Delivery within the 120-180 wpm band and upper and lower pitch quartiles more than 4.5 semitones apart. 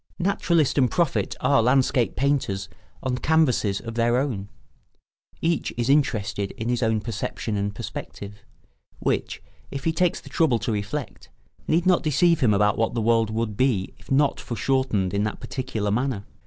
Yes: average, 165 wpm; average, 5.0 semitones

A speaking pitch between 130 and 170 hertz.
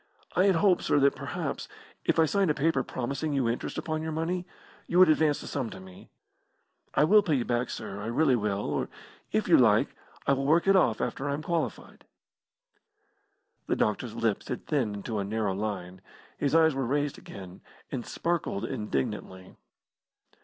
Yes: medium, 140 Hz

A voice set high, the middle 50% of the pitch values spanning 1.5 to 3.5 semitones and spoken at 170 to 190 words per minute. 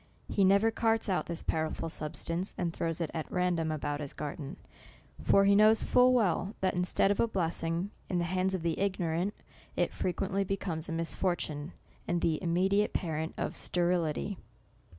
No: medium, 180 Hz; average, 3.1 semitones; average, 175 wpm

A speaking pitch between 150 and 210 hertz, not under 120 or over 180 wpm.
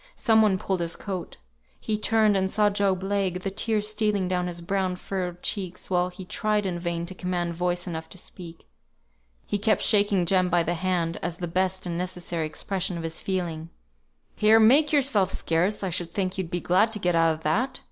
No: medium, 185 Hz; fast, 205 wpm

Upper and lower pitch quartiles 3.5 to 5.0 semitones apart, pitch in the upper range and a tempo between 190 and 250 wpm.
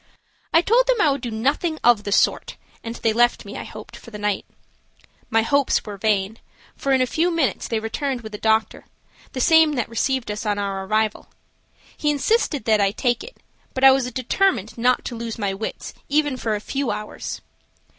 Yes: average, 4.5 semitones; high, 240 Hz; fast, 205 wpm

